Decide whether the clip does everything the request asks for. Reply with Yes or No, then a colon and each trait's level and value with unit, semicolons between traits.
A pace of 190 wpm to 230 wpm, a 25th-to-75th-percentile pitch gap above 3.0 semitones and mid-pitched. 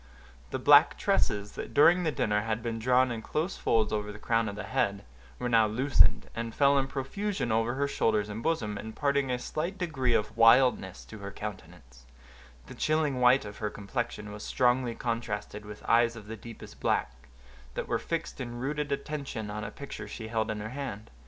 No: average, 195 wpm; average, 4.3 semitones; low, 115 Hz